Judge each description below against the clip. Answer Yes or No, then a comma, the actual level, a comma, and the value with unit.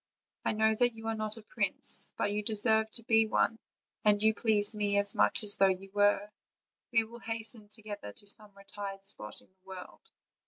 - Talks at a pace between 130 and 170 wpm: No, average, 200 wpm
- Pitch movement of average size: No, narrow, 1.6 semitones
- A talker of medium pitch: No, high, 210 Hz